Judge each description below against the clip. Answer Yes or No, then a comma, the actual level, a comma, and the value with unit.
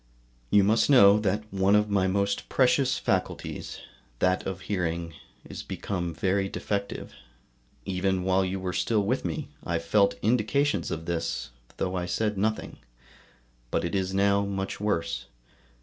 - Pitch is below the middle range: Yes, very low, 95 Hz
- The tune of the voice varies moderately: No, narrow, 2.2 semitones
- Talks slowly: No, average, 150 wpm